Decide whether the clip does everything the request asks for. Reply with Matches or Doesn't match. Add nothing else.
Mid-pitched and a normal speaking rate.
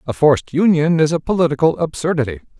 Matches